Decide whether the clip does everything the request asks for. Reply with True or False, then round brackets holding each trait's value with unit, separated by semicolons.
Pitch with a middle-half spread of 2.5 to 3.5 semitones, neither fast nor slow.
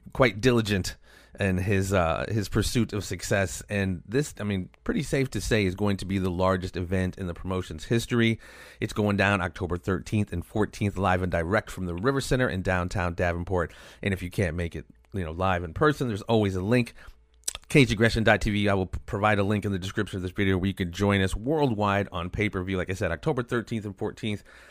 False (3.0 semitones; 210 wpm)